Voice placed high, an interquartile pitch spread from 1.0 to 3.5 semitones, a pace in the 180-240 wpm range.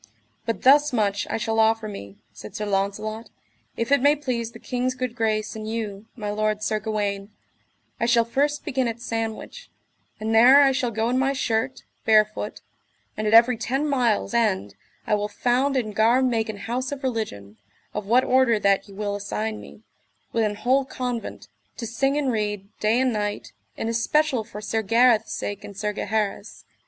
Yes: high, 225 Hz; average, 3.0 semitones; average, 185 wpm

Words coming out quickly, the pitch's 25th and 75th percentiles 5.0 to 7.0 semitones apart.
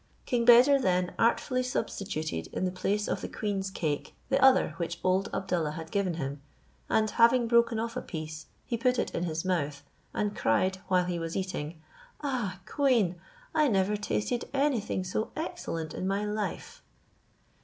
No: average, 165 wpm; wide, 5.4 semitones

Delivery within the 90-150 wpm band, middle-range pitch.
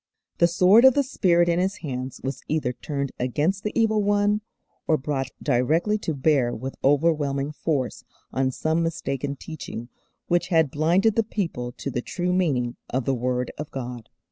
No: average, 170 wpm; medium, 155 Hz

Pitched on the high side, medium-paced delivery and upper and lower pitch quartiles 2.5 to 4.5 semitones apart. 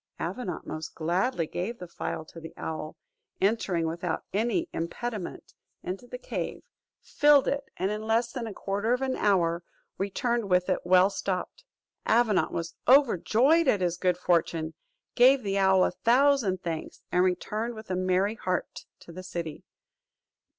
No: high, 195 Hz; average, 155 wpm; average, 5.1 semitones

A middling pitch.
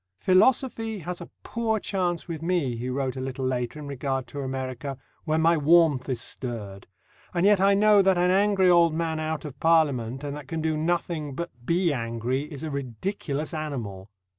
Yes: medium, 155 Hz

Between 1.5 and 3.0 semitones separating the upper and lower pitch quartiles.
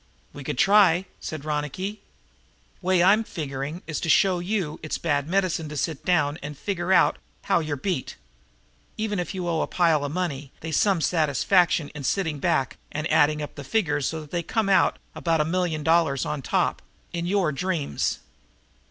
No: average, 3.8 semitones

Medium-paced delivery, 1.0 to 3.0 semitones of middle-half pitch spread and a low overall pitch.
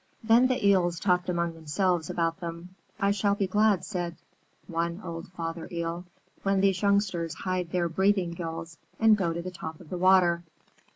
No: average, 175 wpm; narrow, 2.6 semitones; medium, 180 Hz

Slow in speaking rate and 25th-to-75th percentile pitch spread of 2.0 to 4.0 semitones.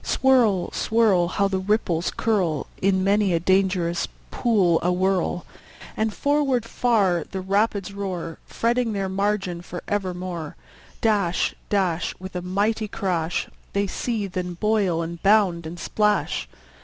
Yes: slow, 130 wpm; average, 3.0 semitones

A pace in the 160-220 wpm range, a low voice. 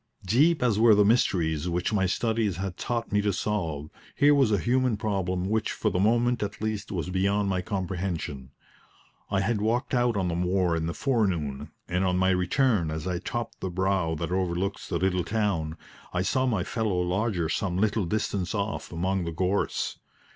Yes: average, 190 wpm; very low, 95 Hz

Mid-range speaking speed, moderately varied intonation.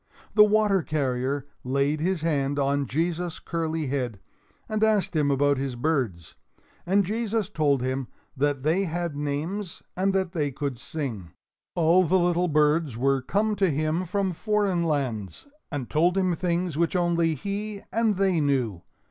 Yes: average, 155 wpm; average, 4.9 semitones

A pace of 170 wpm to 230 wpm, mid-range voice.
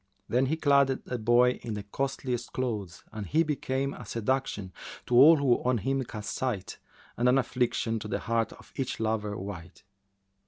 No: average, 180 wpm; low, 120 Hz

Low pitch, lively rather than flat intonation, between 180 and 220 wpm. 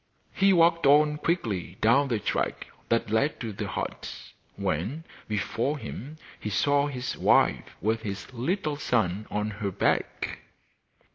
No: low, 120 Hz; wide, 5.9 semitones; average, 140 wpm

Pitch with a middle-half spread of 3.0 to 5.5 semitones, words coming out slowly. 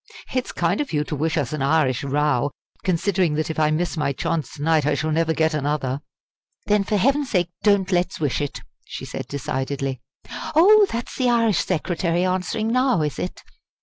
No: average, 5.1 semitones; average, 190 wpm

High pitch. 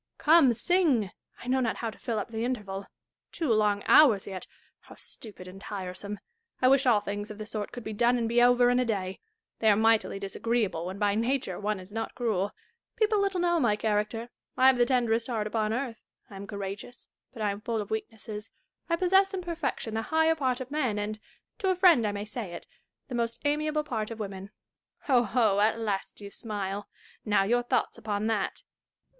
Yes: high, 225 Hz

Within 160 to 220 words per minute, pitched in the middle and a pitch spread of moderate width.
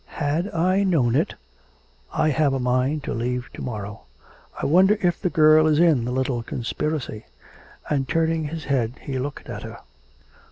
Yes: average, 170 wpm; medium, 145 Hz; average, 4.3 semitones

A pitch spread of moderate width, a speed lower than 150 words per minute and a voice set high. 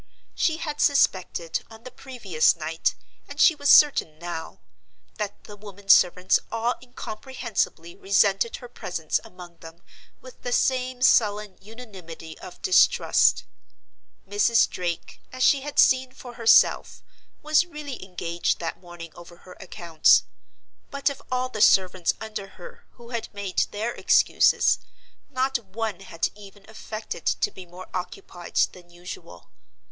No: wide, 6.0 semitones; average, 140 wpm; high, 205 Hz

